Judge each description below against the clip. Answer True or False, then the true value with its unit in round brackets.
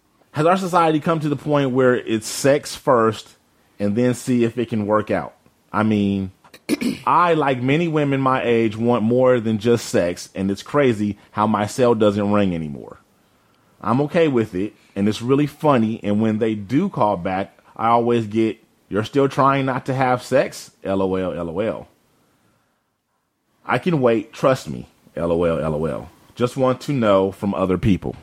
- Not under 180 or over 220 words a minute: False (170 wpm)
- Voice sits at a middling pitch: False (115 Hz)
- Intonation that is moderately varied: True (4.8 semitones)